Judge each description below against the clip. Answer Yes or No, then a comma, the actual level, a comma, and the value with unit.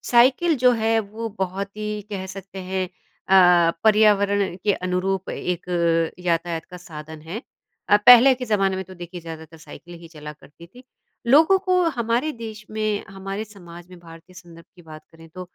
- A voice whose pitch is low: No, high, 190 Hz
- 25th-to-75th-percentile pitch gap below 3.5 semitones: No, average, 3.9 semitones